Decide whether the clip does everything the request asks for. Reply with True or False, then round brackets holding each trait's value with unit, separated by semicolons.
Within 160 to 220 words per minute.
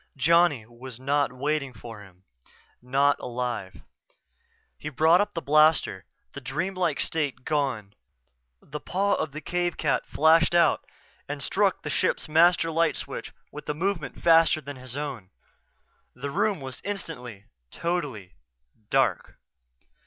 False (140 wpm)